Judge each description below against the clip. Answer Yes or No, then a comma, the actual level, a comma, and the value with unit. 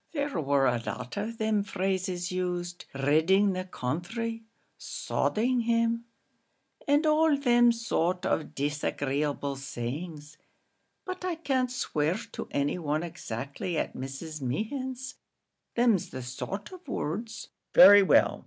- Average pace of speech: No, slow, 125 wpm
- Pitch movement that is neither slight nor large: No, wide, 7.9 semitones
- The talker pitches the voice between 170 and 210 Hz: Yes, medium, 185 Hz